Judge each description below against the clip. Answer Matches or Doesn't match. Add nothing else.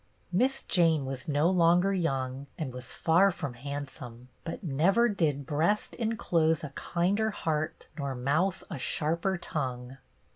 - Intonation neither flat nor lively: Matches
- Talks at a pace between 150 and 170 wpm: Doesn't match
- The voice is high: Doesn't match